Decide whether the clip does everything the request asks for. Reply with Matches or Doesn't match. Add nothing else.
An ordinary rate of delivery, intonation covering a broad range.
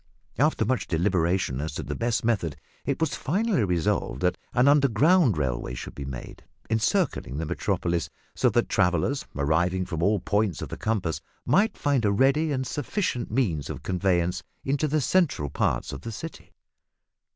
Matches